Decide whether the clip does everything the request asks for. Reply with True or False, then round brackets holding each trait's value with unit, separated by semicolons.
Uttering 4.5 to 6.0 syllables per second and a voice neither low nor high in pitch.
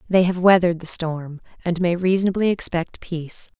True (5.5 syllables/s; 175 Hz)